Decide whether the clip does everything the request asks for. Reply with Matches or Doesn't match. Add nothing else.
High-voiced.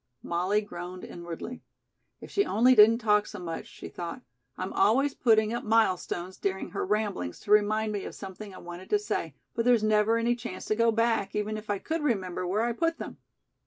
Matches